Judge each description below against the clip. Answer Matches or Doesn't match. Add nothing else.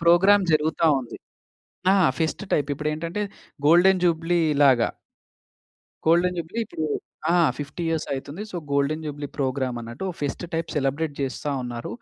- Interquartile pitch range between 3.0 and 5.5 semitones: Matches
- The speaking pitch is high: Doesn't match